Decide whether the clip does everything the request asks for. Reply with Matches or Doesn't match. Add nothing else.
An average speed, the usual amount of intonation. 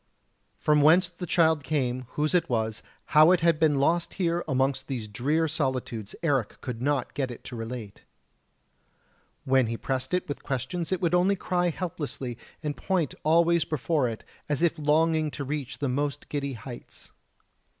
Matches